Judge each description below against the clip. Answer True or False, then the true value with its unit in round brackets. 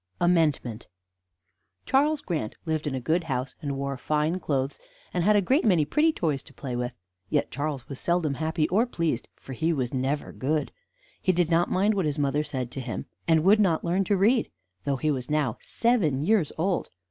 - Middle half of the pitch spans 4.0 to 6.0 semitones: True (4.7 semitones)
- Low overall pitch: False (155 Hz)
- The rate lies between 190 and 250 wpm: True (200 wpm)